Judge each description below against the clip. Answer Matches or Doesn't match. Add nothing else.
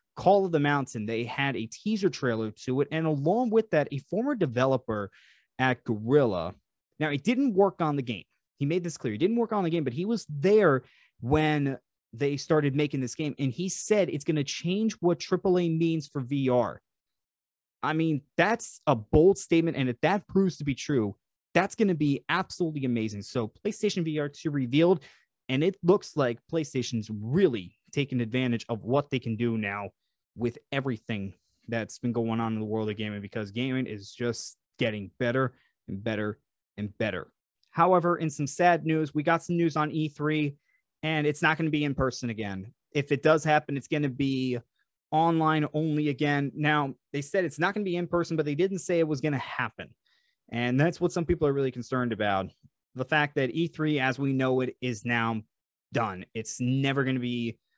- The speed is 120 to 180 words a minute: Doesn't match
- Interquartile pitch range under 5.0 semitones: Doesn't match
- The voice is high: Doesn't match